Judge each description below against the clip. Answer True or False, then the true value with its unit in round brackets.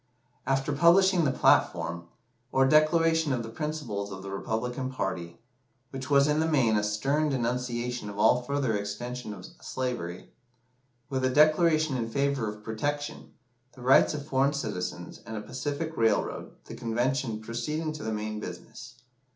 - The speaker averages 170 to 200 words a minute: False (155 wpm)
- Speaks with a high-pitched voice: False (130 Hz)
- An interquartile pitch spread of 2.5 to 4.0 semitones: False (5.0 semitones)